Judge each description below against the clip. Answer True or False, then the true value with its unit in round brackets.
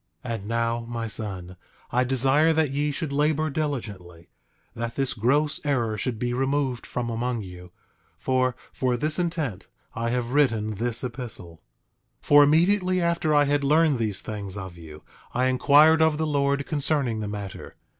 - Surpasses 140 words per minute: True (165 wpm)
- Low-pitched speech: True (130 Hz)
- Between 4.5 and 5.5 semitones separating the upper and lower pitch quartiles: True (4.8 semitones)